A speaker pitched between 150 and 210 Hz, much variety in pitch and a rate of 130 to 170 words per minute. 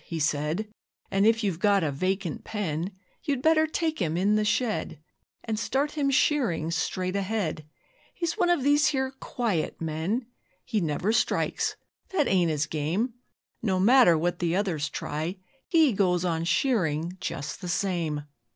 Yes: high, 190 Hz; wide, 6.7 semitones; average, 160 wpm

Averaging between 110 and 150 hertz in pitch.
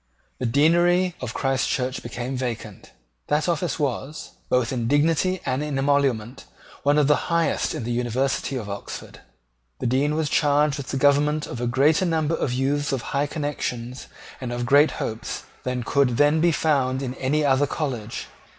Yes: medium, 140 Hz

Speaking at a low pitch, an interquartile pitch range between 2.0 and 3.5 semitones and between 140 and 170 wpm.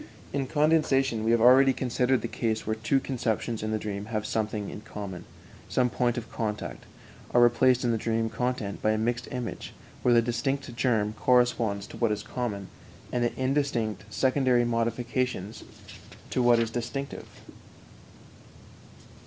Yes: low, 120 Hz; narrow, 2.5 semitones; average, 155 wpm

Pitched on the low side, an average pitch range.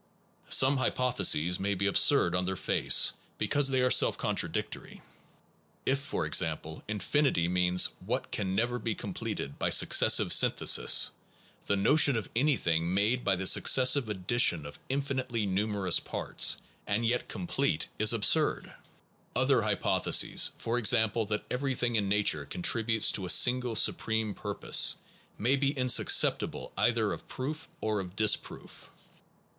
Yes: low, 110 Hz; average, 5.0 semitones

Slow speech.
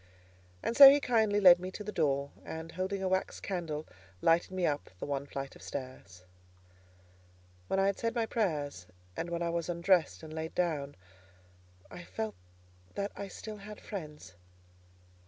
No: average, 170 wpm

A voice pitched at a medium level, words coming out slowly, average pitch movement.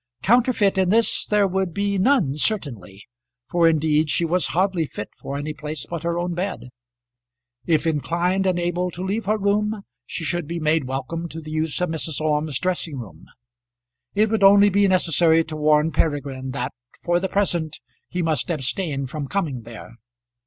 No: medium, 165 Hz; average, 175 wpm; average, 4.0 semitones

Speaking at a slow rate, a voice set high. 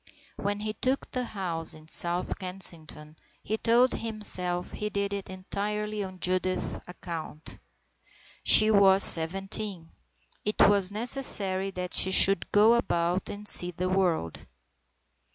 Yes: slow, 130 wpm; high, 195 Hz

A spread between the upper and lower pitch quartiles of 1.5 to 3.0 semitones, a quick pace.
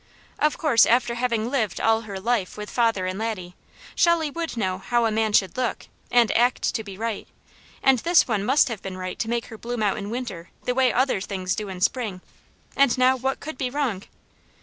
No: average, 4.1 semitones; fast, 215 wpm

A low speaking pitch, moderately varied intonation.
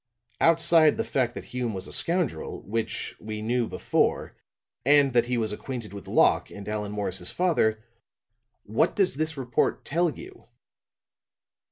No: low, 120 Hz; wide, 6.6 semitones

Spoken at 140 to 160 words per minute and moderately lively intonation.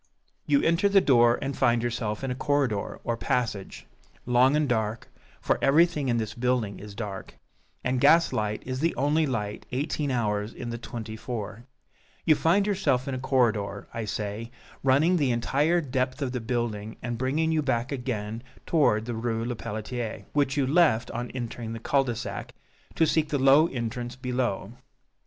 No: average, 175 wpm; average, 3.8 semitones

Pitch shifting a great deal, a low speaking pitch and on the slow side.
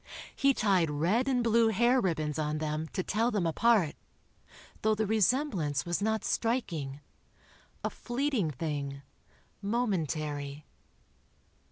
No: wide, 7.2 semitones; high, 190 Hz; slow, 120 wpm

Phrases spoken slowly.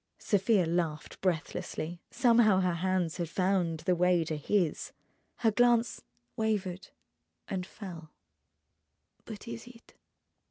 Yes: slow, 115 wpm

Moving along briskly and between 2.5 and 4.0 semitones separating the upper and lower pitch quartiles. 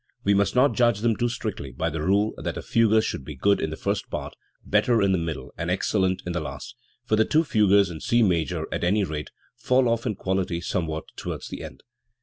No: fast, 235 wpm; average, 4.7 semitones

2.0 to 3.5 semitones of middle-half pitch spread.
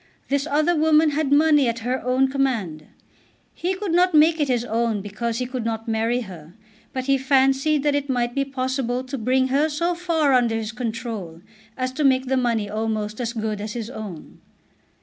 No: average, 4.0 semitones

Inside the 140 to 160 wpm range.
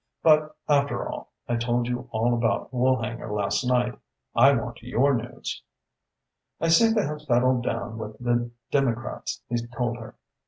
Yes: average, 155 wpm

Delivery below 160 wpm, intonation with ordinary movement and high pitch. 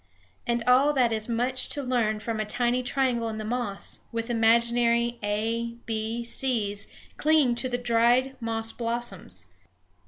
No: average, 150 wpm; narrow, 1.7 semitones; high, 235 Hz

